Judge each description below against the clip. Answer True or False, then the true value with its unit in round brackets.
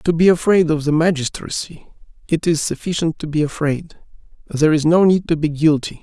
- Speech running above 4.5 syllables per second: True (5.5 syllables/s)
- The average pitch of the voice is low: False (160 Hz)